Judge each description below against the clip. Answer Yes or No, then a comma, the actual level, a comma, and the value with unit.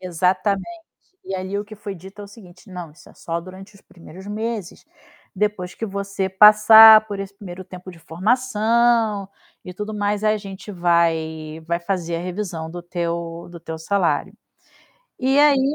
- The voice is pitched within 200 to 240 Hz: No, high, 190 Hz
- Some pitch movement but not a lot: Yes, average, 3.3 semitones